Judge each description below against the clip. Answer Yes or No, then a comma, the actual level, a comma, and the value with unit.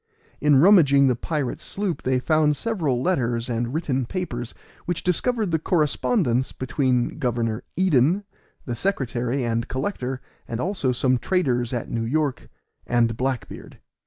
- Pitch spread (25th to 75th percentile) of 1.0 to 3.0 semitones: No, wide, 5.4 semitones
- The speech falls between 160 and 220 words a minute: No, average, 140 wpm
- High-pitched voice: No, low, 130 Hz